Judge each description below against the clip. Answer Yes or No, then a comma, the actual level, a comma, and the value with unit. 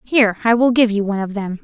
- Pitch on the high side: Yes, high, 215 Hz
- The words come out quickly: Yes, fast, 295 wpm